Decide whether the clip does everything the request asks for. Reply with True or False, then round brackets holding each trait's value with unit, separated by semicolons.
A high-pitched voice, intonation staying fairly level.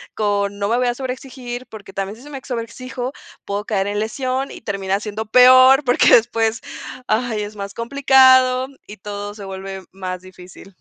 False (220 Hz; 4.1 semitones)